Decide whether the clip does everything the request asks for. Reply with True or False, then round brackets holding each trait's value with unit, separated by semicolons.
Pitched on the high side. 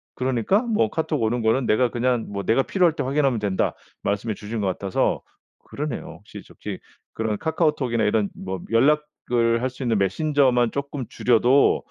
False (120 Hz)